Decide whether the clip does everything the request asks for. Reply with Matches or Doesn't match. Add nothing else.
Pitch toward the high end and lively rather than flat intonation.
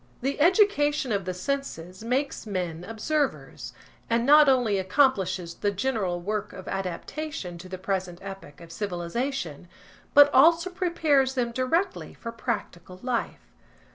Matches